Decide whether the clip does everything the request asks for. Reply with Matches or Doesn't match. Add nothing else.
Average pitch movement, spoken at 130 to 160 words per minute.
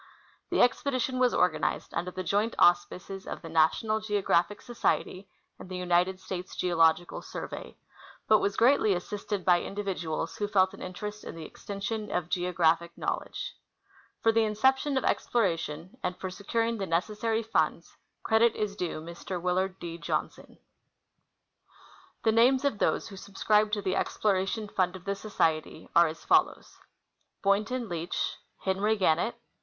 Matches